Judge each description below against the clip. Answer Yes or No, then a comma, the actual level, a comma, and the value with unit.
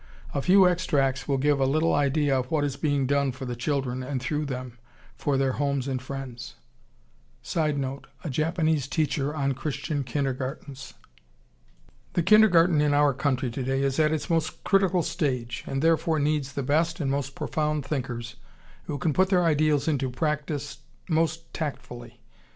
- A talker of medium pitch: Yes, medium, 145 Hz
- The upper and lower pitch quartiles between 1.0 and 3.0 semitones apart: Yes, average, 2.7 semitones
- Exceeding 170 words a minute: No, average, 160 wpm